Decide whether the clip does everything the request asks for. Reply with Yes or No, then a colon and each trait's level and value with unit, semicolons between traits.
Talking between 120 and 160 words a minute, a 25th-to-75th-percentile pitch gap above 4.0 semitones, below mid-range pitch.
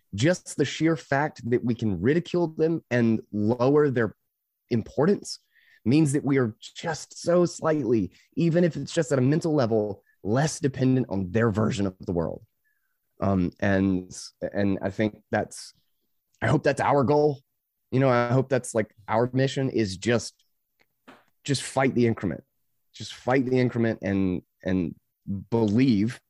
Yes: average, 155 wpm; average, 5.2 semitones; low, 120 Hz